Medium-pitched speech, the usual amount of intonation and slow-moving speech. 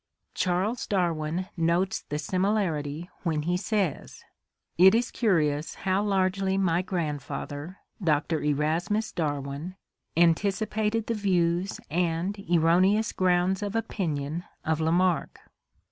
Yes: medium, 180 Hz; average, 3.5 semitones; slow, 110 wpm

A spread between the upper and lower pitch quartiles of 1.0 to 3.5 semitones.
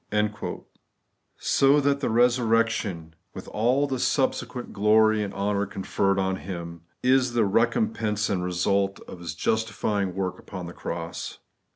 No: average, 3.9 semitones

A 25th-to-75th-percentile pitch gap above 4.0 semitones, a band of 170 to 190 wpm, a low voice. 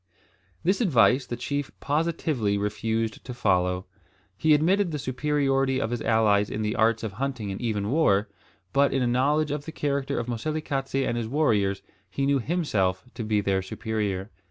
Yes: average, 5.2 semitones; average, 175 wpm; low, 120 Hz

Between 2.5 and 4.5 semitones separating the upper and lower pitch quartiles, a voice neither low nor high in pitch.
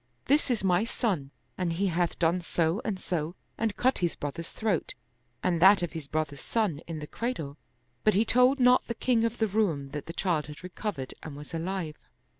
No: wide, 5.6 semitones; medium, 180 Hz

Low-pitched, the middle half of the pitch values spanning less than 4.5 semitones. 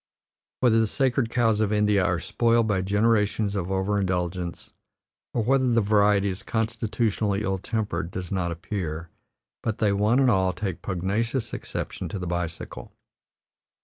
Yes: low, 105 Hz; average, 3.3 semitones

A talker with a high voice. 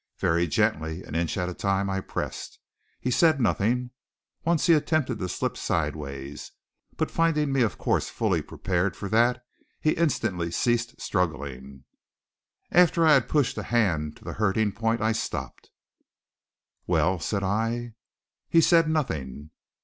No: low, 110 Hz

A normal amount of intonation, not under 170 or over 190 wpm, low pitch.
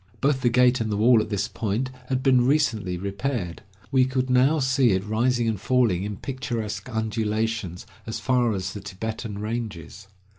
Yes: average, 3.7 semitones; average, 175 wpm; low, 115 Hz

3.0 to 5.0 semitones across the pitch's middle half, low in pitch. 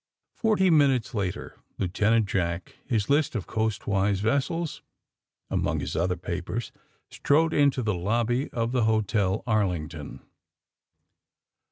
No: wide, 5.4 semitones; low, 110 Hz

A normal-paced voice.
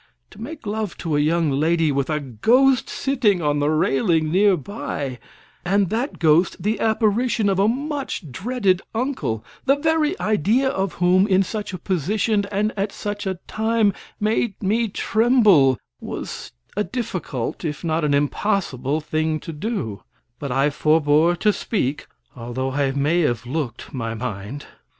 Yes: average, 155 wpm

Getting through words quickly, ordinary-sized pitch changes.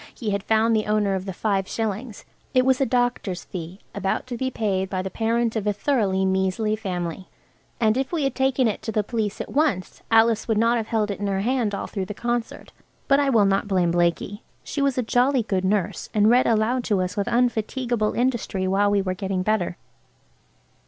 Yes: fast, 215 wpm; average, 3.8 semitones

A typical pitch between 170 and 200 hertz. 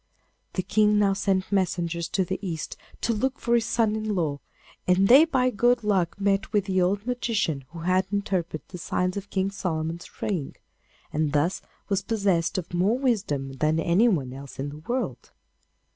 Yes: high, 190 Hz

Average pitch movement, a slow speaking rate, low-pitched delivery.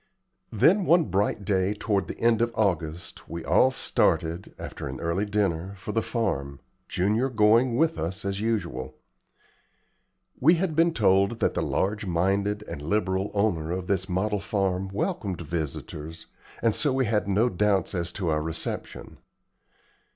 No: average, 4.1 semitones; average, 155 wpm; low, 100 Hz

